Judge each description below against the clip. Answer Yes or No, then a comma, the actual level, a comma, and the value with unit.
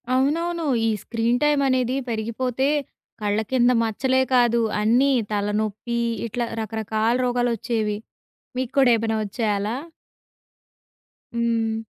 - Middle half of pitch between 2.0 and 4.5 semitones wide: Yes, narrow, 2.6 semitones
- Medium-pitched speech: No, high, 235 Hz